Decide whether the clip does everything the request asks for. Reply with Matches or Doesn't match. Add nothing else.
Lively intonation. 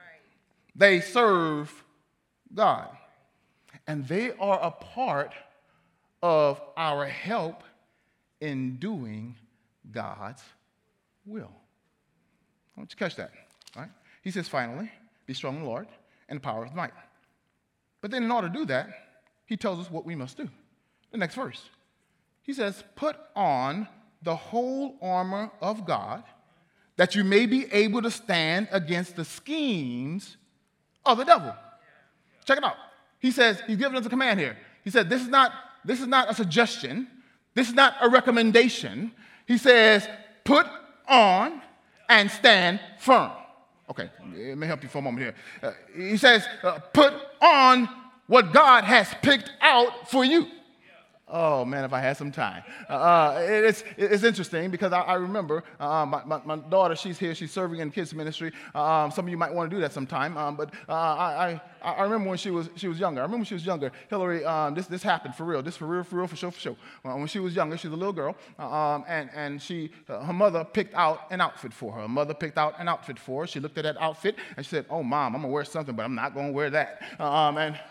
Matches